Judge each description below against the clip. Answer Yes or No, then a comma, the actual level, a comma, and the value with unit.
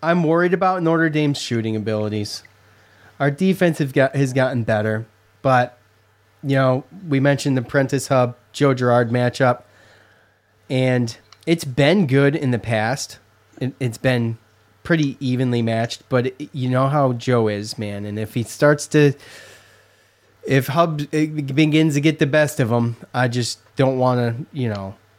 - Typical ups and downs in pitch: Yes, average, 4.5 semitones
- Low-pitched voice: Yes, low, 125 Hz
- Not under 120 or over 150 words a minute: No, average, 160 wpm